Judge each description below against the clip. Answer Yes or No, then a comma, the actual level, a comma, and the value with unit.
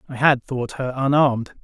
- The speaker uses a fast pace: No, average, 185 wpm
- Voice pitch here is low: Yes, low, 130 Hz